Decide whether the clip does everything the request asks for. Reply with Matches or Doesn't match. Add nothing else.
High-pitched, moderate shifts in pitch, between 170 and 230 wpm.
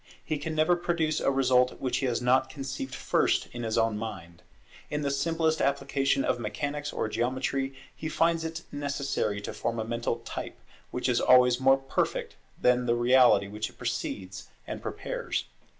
Doesn't match